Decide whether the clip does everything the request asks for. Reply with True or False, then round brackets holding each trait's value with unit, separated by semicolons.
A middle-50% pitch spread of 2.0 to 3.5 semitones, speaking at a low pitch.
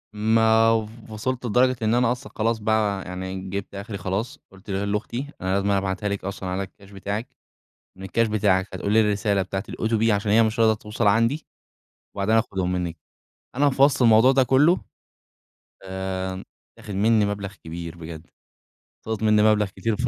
True (2.9 semitones; 105 Hz)